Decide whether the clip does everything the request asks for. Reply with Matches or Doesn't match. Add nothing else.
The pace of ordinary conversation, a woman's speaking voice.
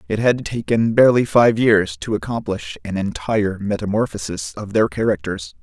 Doesn't match